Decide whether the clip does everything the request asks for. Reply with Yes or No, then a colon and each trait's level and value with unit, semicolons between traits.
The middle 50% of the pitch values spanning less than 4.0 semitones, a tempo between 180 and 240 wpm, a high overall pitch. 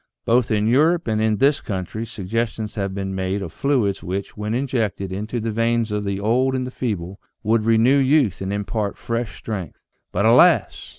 No: average, 3.2 semitones; average, 185 wpm; low, 110 Hz